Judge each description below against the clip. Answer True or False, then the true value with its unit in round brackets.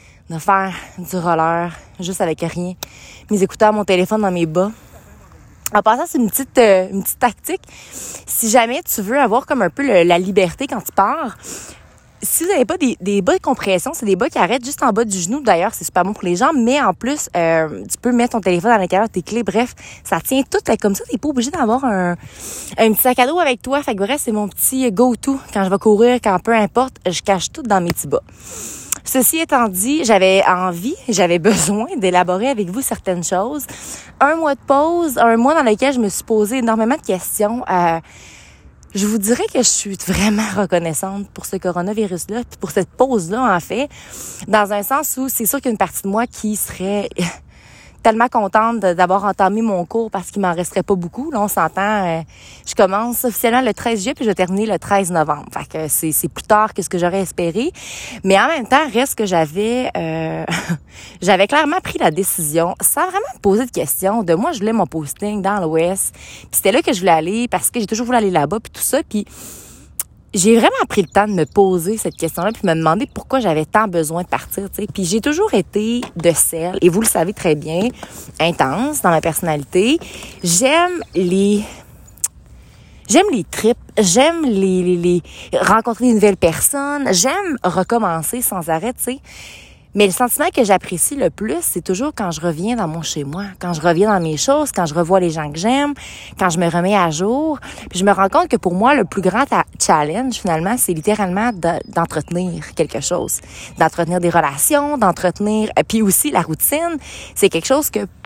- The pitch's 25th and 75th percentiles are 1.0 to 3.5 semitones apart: False (5.4 semitones)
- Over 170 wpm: True (210 wpm)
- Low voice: False (205 Hz)